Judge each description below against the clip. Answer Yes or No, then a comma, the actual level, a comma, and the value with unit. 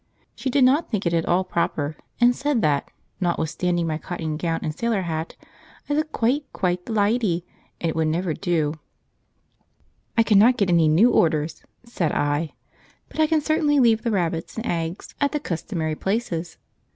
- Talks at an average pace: Yes, average, 175 wpm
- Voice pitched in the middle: Yes, medium, 180 Hz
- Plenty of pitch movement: Yes, wide, 6.4 semitones